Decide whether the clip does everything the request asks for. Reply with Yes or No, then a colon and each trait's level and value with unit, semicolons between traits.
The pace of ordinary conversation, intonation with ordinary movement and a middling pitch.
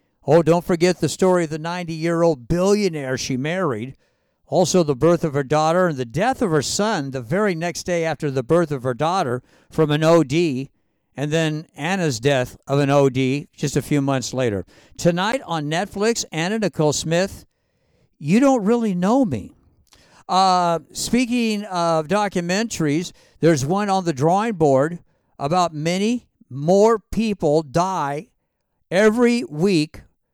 Yes: average, 155 wpm; average, 4.4 semitones; medium, 170 Hz